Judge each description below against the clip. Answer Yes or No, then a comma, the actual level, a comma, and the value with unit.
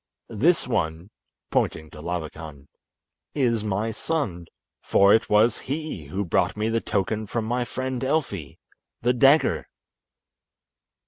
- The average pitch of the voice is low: Yes, low, 110 Hz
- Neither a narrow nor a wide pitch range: No, wide, 6.3 semitones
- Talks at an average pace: No, slow, 120 wpm